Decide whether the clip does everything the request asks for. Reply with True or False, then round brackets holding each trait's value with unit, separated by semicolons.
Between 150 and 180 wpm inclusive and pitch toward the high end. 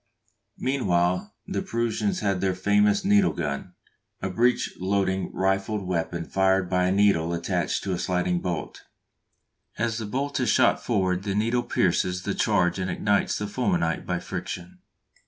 False (155 wpm; 95 Hz)